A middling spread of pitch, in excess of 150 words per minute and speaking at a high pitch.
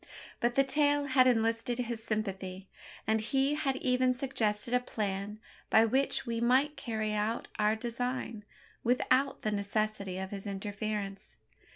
No: average, 3.4 semitones; average, 145 wpm; high, 225 Hz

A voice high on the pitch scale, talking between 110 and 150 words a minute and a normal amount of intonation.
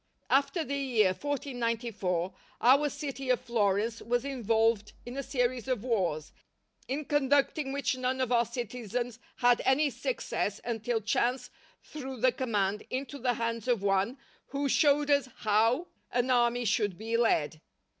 Yes: high, 245 Hz; average, 145 wpm; average, 3.3 semitones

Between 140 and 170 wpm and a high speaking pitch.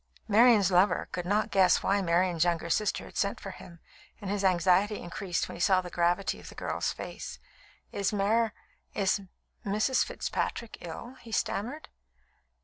Yes: average, 160 wpm; high, 195 Hz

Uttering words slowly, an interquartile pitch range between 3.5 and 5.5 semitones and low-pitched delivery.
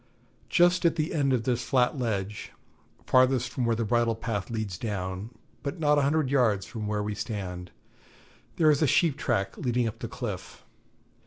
No: average, 180 wpm; average, 5.0 semitones; low, 120 Hz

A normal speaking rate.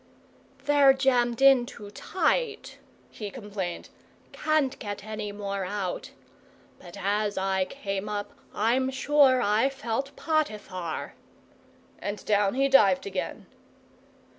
No: slow, 115 wpm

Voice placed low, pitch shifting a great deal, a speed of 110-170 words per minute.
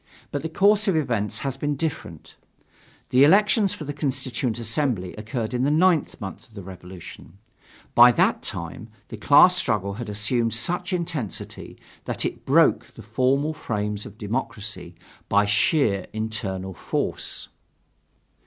Yes: low, 120 Hz; wide, 6.1 semitones; average, 145 wpm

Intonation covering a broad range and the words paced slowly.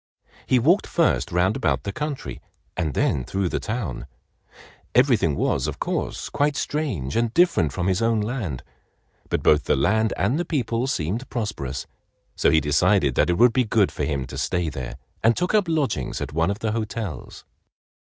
No: wide, 7.9 semitones; average, 180 wpm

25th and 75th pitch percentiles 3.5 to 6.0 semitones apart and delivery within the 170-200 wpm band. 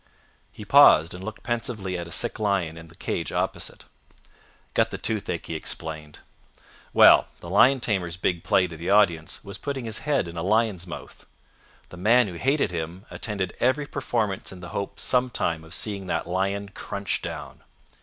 Yes: average, 4.3 semitones; average, 175 wpm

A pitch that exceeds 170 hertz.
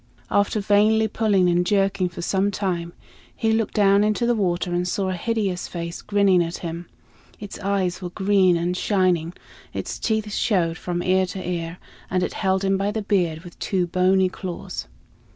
Yes: high, 190 Hz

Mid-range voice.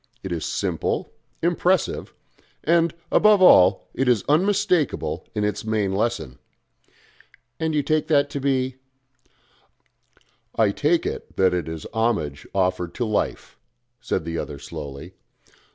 No: low, 115 Hz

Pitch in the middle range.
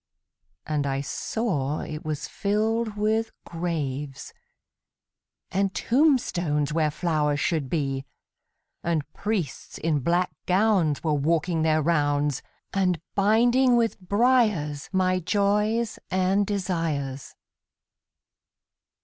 Yes: medium, 170 Hz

